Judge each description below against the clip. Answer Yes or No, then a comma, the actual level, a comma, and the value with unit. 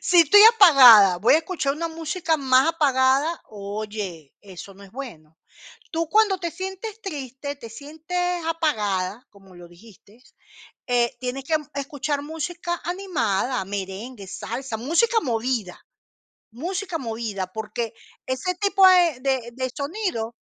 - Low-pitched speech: No, very high, 265 Hz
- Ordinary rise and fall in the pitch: No, wide, 7.3 semitones